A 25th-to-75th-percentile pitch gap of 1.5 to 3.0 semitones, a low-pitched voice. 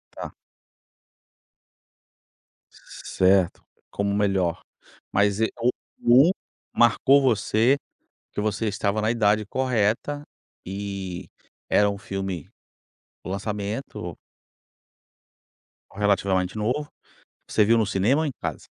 Yes: average, 2.7 semitones; low, 105 Hz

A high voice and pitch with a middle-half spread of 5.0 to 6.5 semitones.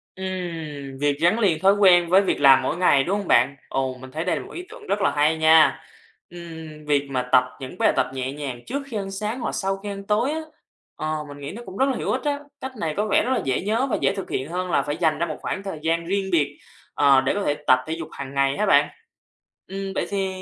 No: medium, 170 Hz; wide, 5.6 semitones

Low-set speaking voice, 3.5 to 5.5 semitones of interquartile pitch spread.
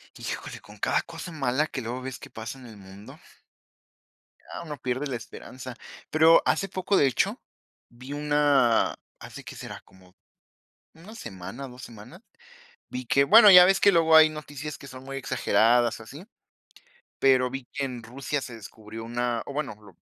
Yes: low, 130 Hz; average, 4.0 semitones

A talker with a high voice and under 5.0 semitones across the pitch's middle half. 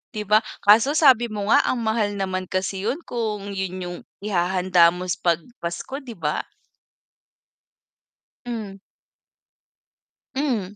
Yes: high, 205 Hz; average, 3.7 semitones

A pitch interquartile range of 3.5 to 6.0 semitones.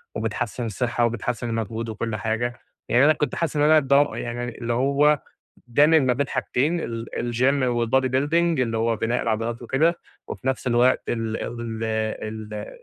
No: average, 3.1 semitones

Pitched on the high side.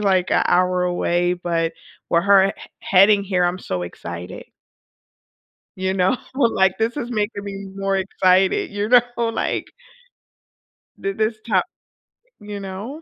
Yes: high, 195 Hz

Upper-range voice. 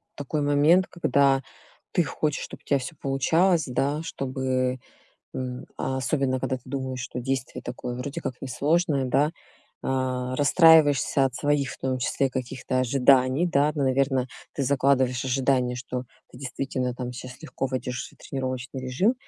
No: low, 130 Hz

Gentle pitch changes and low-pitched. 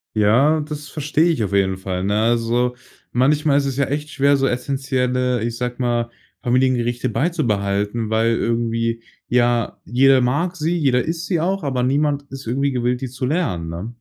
No: average, 3.6 semitones; low, 125 Hz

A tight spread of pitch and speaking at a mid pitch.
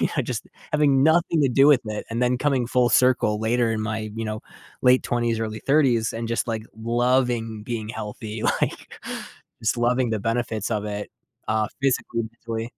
No: narrow, 2.3 semitones; low, 115 Hz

